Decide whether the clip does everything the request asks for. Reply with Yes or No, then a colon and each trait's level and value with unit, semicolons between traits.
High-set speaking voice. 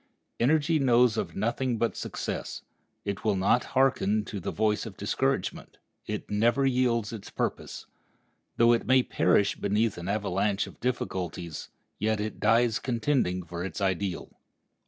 No: low, 110 Hz